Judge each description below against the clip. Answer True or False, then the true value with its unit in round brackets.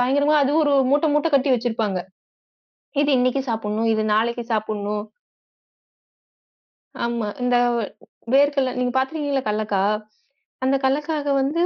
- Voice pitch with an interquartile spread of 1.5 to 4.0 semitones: False (4.5 semitones)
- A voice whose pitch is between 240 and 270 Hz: True (250 Hz)